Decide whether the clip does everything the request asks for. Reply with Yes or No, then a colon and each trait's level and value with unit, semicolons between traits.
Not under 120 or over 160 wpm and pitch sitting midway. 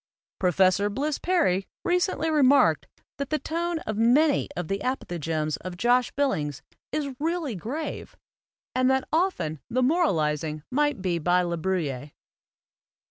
No: slow, 135 wpm; high, 235 Hz